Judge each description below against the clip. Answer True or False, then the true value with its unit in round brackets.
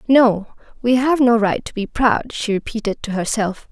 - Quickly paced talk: False (195 wpm)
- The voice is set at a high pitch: True (225 Hz)